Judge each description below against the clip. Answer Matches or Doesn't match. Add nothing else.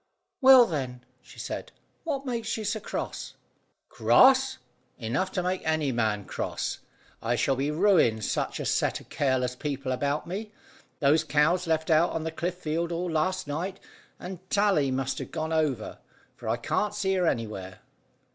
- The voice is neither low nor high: Matches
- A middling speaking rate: Matches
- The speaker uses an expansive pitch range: Matches